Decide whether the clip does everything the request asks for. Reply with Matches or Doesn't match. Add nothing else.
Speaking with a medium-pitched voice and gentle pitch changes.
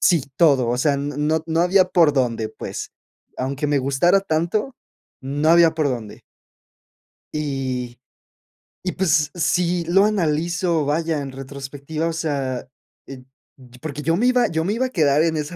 Doesn't match